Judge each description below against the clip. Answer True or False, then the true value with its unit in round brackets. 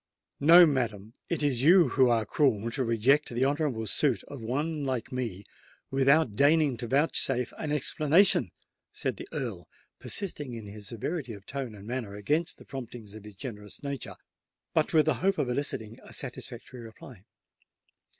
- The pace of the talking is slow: False (160 wpm)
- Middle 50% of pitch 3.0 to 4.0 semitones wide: False (4.6 semitones)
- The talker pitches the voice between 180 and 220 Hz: False (130 Hz)